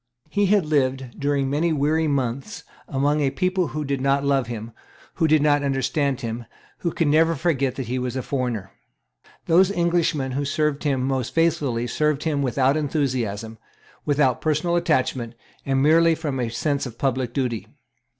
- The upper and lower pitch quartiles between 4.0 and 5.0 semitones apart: No, average, 3.2 semitones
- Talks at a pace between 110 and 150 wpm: No, average, 170 wpm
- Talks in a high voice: No, medium, 140 Hz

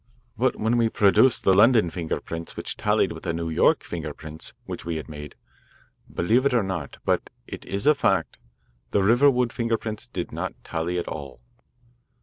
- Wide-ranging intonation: Yes, wide, 6.1 semitones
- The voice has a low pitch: Yes, very low, 95 Hz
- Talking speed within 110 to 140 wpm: No, average, 185 wpm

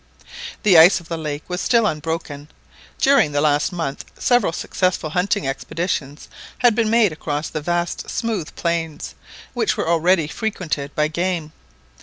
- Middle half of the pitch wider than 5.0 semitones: No, average, 3.7 semitones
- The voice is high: No, medium, 165 Hz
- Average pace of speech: Yes, average, 150 wpm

